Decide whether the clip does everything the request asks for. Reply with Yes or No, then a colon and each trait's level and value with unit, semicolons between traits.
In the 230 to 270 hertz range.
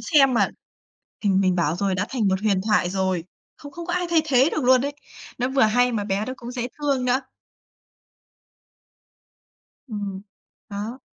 Yes: high, 235 Hz